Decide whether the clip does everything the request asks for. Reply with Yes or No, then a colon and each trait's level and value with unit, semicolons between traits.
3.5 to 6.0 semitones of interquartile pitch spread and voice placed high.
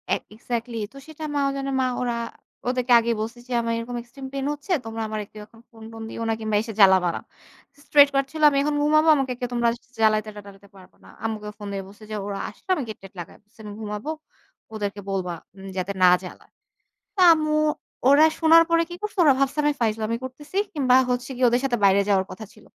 Yes: average, 4.7 semitones; high, 230 Hz